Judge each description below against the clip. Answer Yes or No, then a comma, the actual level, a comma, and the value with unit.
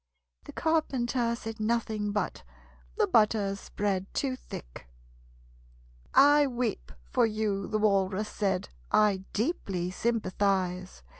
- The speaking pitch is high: Yes, high, 210 Hz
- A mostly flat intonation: No, average, 3.4 semitones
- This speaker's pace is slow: Yes, slow, 105 wpm